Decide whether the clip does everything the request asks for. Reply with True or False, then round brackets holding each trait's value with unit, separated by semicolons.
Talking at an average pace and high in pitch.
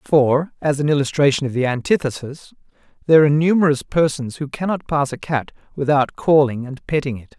False (170 wpm; 145 Hz)